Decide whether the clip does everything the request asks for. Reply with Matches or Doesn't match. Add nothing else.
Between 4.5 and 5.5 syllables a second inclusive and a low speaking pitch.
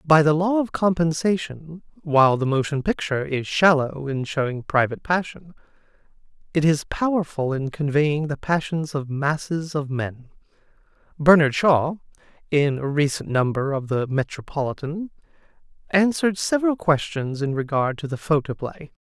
Doesn't match